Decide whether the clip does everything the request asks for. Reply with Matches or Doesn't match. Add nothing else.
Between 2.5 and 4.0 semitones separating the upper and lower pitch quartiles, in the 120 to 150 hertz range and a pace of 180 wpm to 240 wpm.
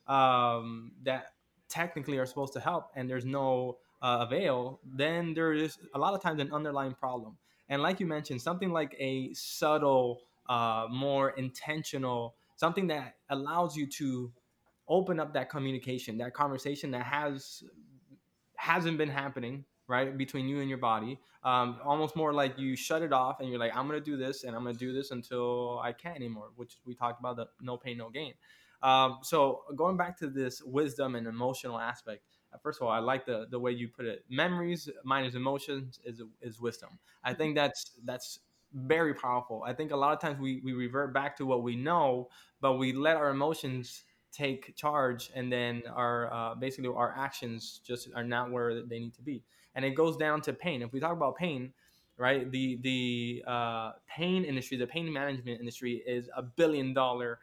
Matches